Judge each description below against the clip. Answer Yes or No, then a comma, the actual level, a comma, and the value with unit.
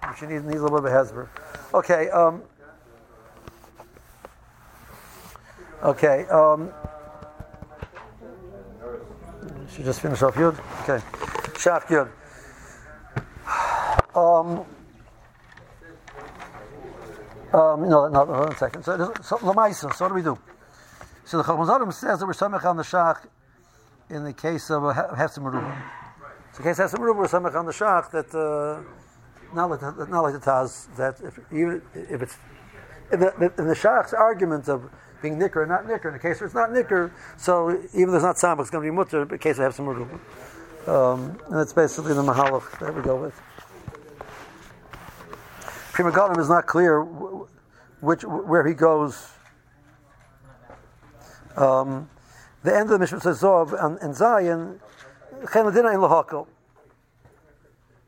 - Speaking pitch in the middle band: Yes, medium, 155 Hz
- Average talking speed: Yes, average, 145 wpm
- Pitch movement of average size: Yes, average, 4.5 semitones